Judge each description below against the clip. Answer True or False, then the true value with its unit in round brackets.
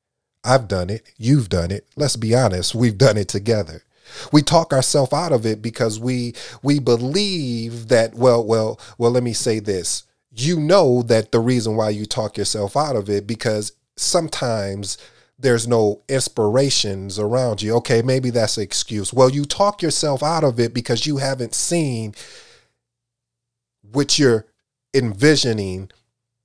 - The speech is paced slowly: False (155 wpm)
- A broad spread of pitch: False (3.5 semitones)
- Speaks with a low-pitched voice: True (120 Hz)